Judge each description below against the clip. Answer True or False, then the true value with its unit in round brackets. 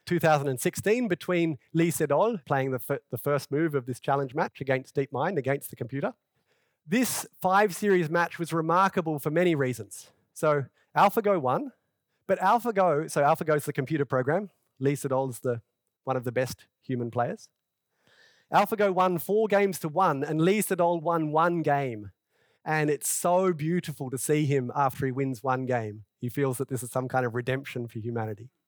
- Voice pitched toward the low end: False (150 Hz)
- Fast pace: False (175 wpm)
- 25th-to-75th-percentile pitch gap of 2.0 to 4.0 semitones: False (5.2 semitones)